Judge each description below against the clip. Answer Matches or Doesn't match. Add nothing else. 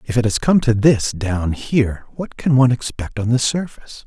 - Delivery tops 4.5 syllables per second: Matches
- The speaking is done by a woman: Doesn't match